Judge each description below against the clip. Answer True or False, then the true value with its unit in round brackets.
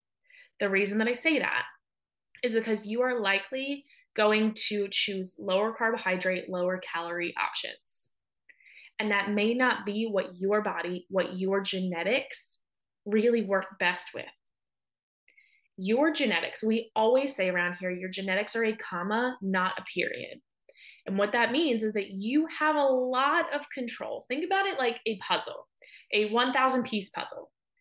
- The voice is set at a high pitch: True (220 Hz)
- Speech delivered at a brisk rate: False (155 wpm)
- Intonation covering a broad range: False (4.8 semitones)